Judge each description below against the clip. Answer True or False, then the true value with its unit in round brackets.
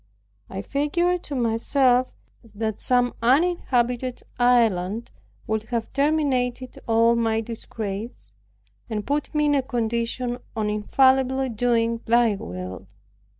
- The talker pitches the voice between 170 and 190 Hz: False (240 Hz)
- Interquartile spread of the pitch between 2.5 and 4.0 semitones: True (2.8 semitones)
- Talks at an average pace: False (110 wpm)